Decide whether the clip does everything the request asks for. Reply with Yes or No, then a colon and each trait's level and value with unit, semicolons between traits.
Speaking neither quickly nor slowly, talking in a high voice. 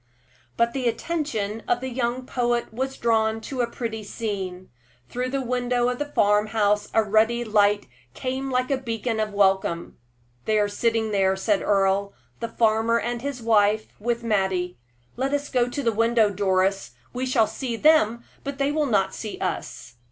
Yes: average, 175 wpm; high, 225 Hz